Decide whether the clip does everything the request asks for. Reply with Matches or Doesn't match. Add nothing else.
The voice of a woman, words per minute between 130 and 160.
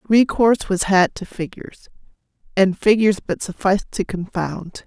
Matches